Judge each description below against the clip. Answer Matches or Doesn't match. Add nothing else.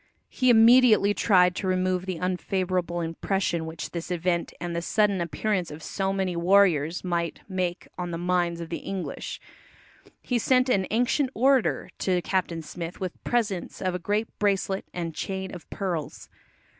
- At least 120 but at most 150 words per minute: Doesn't match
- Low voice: Doesn't match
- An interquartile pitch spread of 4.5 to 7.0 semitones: Doesn't match